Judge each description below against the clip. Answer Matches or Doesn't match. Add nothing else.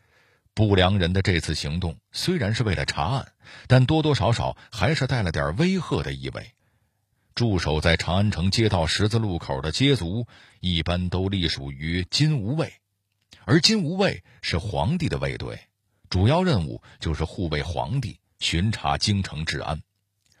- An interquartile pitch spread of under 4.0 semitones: Doesn't match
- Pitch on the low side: Matches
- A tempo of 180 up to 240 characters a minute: Matches